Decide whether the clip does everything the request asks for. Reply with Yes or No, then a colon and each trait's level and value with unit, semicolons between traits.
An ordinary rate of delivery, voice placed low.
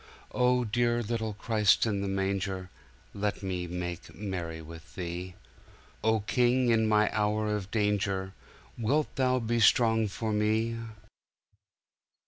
No: slow, 120 wpm; low, 105 Hz